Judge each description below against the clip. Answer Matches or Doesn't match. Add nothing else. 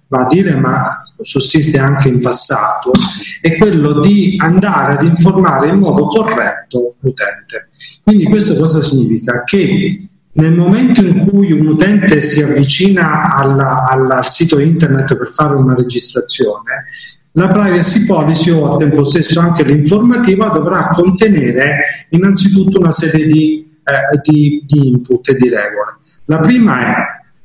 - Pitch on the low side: Doesn't match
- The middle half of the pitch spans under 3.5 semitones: Doesn't match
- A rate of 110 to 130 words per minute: Doesn't match